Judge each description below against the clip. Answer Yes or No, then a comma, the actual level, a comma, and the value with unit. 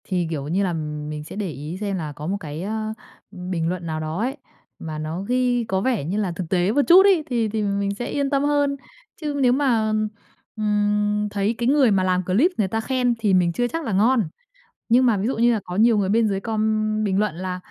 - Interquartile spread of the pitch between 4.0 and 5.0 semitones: Yes, average, 4.7 semitones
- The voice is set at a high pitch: Yes, high, 210 Hz